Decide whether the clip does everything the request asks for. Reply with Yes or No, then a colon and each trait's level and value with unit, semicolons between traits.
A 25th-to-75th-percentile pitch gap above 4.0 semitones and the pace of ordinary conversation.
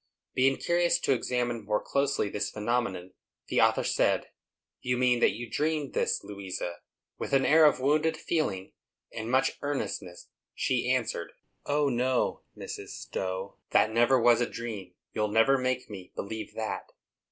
Yes: average, 4.4 semitones; average, 155 wpm